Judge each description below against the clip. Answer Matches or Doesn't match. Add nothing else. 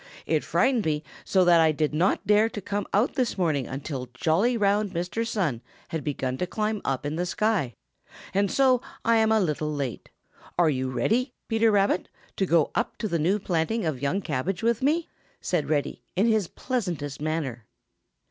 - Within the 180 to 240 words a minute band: Matches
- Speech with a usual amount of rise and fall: Doesn't match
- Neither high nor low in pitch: Matches